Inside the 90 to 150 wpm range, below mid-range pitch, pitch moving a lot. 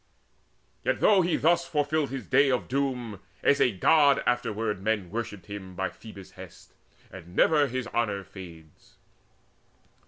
Yes: average, 145 wpm; low, 115 Hz; wide, 6.1 semitones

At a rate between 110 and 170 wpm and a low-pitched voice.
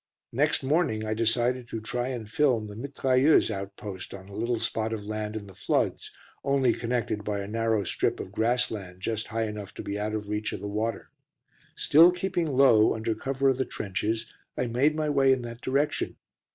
No: average, 200 wpm; low, 115 Hz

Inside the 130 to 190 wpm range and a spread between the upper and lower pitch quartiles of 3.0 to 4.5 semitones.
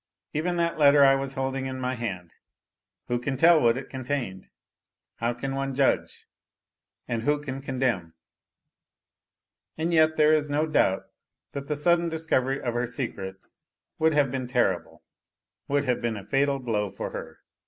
Yes: average, 165 wpm; average, 3.5 semitones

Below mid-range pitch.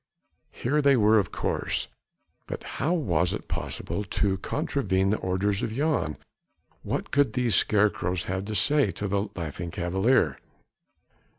Yes: low, 100 Hz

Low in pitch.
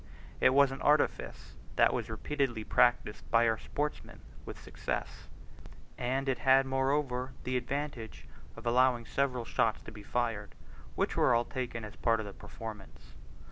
Yes: low, 125 Hz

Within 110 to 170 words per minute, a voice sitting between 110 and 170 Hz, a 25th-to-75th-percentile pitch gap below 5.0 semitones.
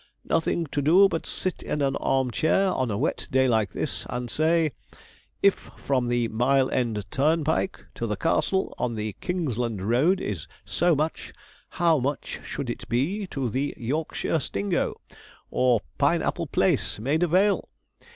No: average, 160 wpm; low, 135 Hz; wide, 5.4 semitones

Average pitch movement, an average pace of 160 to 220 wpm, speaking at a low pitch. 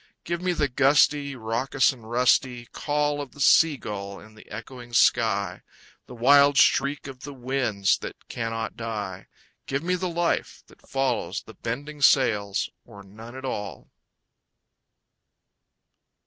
No: average, 4.3 semitones; average, 140 wpm; low, 125 Hz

